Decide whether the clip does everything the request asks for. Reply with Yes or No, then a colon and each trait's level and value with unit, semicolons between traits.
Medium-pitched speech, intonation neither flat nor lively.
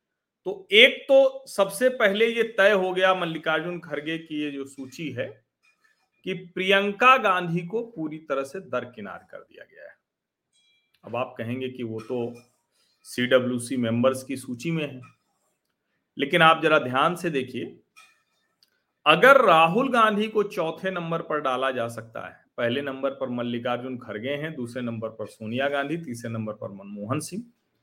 No: medium, 155 Hz; wide, 7.6 semitones